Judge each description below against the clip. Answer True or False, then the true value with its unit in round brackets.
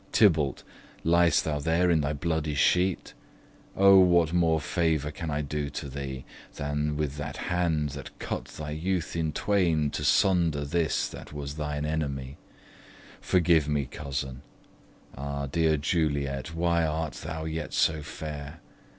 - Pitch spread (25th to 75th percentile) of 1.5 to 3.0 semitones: True (2.6 semitones)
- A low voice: True (75 Hz)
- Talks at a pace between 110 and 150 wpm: True (145 wpm)